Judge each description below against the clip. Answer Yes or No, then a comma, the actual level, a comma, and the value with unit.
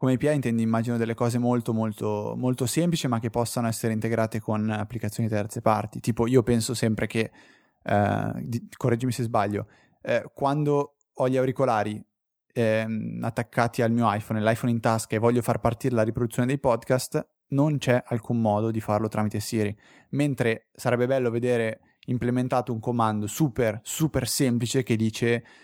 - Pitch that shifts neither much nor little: No, narrow, 2.1 semitones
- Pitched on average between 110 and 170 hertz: Yes, low, 120 Hz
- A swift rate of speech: No, average, 160 wpm